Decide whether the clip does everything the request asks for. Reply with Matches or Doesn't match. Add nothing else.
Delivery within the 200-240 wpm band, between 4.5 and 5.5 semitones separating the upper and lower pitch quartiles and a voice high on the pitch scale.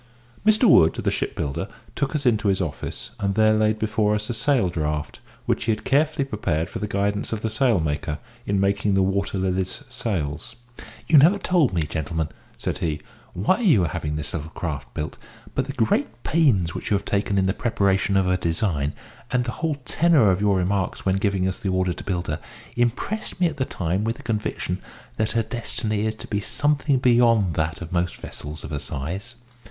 Doesn't match